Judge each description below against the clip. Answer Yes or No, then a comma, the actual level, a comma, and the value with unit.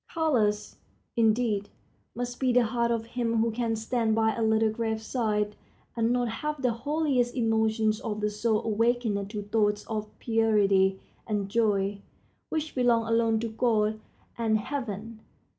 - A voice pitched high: Yes, high, 225 Hz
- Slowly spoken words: No, average, 150 wpm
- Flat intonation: Yes, narrow, 2.0 semitones